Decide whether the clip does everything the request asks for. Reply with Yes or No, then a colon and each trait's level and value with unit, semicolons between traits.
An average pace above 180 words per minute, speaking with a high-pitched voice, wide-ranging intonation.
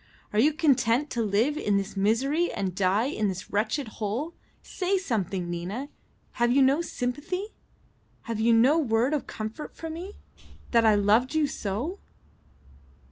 No: average, 155 wpm; high, 235 Hz; wide, 6.2 semitones